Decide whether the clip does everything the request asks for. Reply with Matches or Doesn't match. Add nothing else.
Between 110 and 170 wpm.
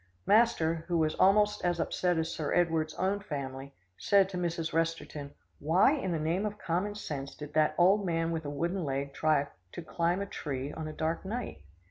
Doesn't match